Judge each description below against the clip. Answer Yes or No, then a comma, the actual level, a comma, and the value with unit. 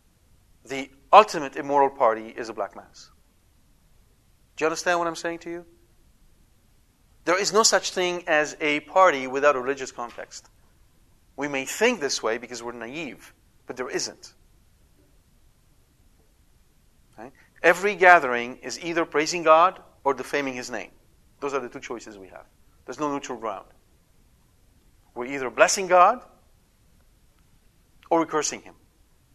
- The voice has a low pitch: Yes, low, 130 Hz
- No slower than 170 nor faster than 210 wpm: No, average, 140 wpm